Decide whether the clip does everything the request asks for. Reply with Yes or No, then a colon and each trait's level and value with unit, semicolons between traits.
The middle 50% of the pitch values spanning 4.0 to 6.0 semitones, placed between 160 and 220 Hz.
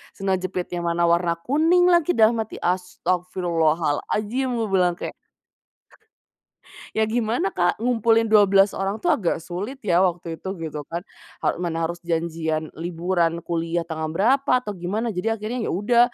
Yes: average, 4.6 semitones; medium, 185 Hz